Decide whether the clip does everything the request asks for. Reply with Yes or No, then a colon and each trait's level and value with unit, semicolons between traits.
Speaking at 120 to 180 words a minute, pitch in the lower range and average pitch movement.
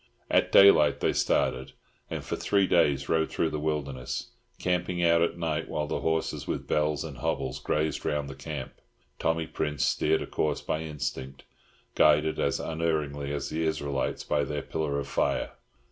No: average, 170 wpm; very low, 75 Hz; narrow, 2.2 semitones